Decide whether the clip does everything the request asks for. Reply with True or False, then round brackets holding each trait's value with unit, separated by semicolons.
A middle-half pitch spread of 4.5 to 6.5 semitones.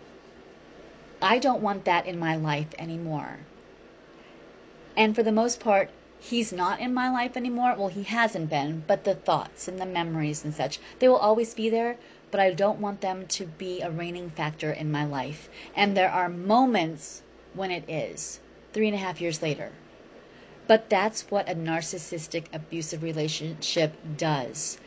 True (4.9 semitones)